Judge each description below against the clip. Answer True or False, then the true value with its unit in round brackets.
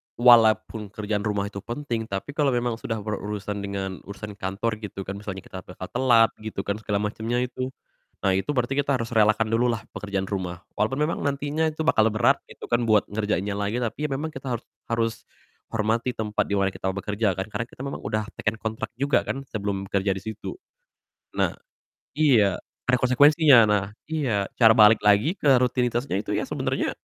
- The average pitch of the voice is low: True (110 Hz)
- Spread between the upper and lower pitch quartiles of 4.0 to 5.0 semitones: False (3.4 semitones)